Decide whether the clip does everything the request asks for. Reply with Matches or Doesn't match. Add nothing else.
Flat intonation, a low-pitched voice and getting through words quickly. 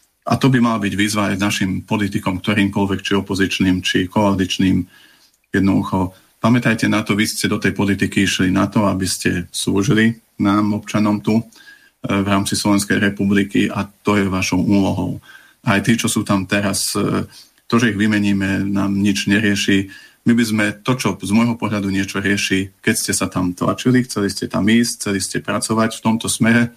Matches